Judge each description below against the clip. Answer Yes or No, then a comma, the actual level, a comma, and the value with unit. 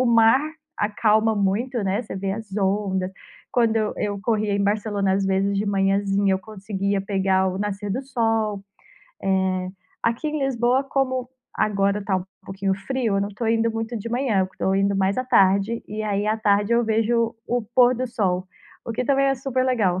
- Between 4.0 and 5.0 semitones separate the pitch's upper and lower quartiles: No, average, 3.0 semitones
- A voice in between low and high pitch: No, high, 210 Hz